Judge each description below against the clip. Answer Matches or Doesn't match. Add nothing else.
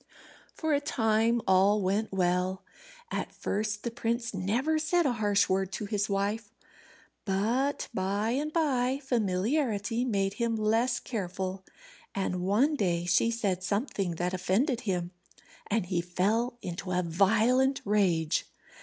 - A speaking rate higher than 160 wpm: Doesn't match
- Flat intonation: Doesn't match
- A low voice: Doesn't match